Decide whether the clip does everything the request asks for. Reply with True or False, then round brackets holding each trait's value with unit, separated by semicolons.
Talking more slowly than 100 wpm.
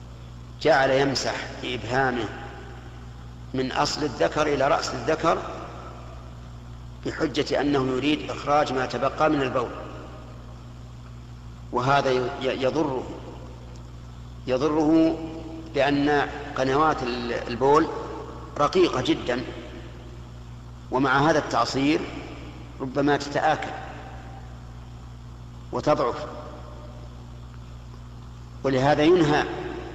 True (70 wpm)